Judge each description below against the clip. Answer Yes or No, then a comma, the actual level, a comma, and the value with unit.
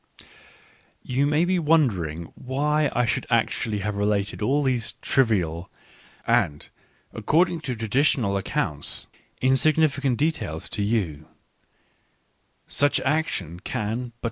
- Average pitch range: No, wide, 6.4 semitones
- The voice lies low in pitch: Yes, low, 125 Hz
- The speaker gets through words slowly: Yes, slow, 115 wpm